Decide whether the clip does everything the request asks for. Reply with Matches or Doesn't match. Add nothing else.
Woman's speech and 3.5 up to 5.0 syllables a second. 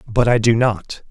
Doesn't match